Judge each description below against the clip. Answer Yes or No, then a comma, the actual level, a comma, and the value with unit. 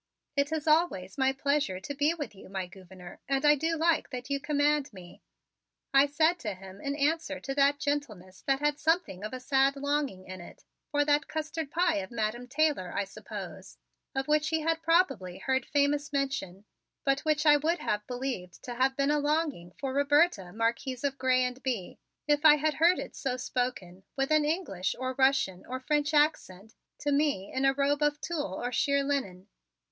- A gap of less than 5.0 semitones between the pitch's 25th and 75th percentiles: Yes, average, 4.5 semitones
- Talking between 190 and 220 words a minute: Yes, average, 195 wpm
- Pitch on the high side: Yes, very high, 275 Hz